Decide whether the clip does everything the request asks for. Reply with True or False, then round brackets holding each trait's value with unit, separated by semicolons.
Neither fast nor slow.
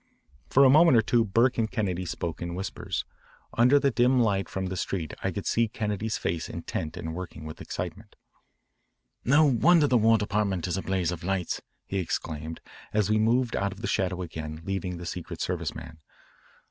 True (190 wpm)